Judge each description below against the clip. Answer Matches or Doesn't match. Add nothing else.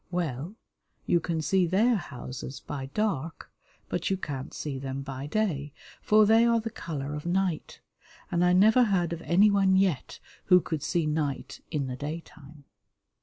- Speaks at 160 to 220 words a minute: Matches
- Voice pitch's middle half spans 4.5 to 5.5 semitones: Matches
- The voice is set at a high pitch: Doesn't match